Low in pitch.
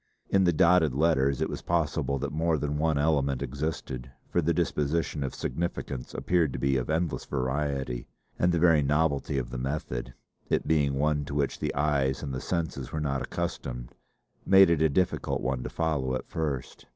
Yes: very low, 75 Hz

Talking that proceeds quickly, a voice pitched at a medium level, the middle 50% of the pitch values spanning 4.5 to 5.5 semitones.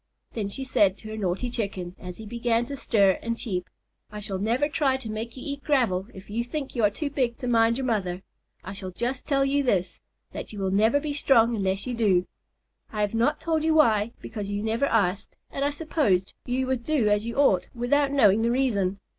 No: fast, 225 wpm; high, 230 Hz; average, 4.8 semitones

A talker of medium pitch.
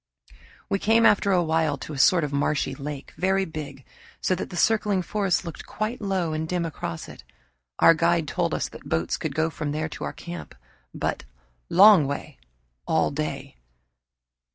Yes: medium, 165 Hz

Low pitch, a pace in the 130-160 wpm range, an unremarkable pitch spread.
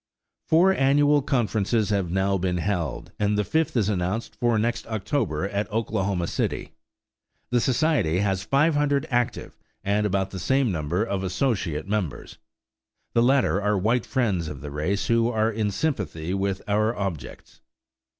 Yes: low, 105 Hz; average, 150 wpm; average, 4.2 semitones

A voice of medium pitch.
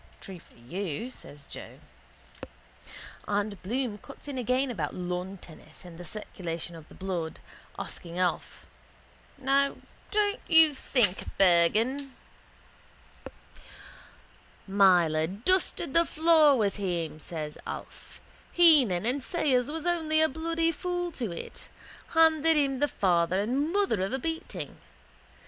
No: high, 235 Hz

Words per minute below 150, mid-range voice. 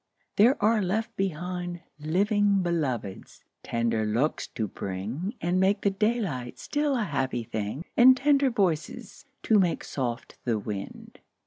Yes: slow, 135 wpm; medium, 175 Hz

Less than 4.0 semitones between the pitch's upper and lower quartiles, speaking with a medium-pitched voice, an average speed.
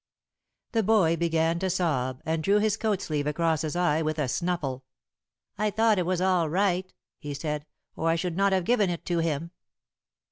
Yes: average, 3.3 semitones; medium, 170 Hz; average, 190 wpm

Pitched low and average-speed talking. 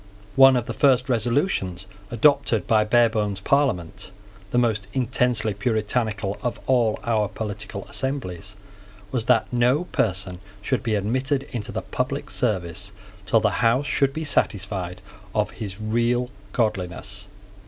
No: low, 115 Hz; slow, 130 wpm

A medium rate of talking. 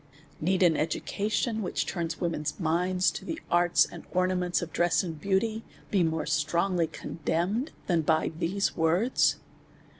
Yes: average, 145 wpm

